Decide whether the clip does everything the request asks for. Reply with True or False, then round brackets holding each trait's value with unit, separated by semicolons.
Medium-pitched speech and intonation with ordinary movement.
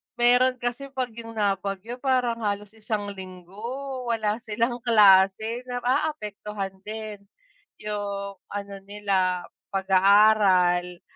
False (210 Hz; 3.3 semitones)